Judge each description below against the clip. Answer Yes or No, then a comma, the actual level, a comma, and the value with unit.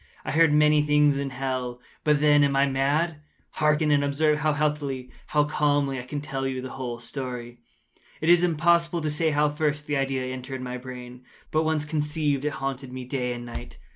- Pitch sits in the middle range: Yes, medium, 145 Hz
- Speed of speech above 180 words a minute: Yes, average, 195 wpm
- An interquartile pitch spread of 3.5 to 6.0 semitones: No, narrow, 2.6 semitones